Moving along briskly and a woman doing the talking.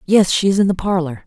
Yes: fast, 285 wpm; female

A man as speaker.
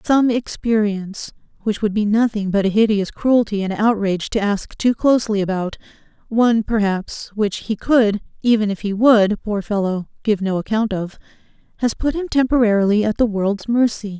No: female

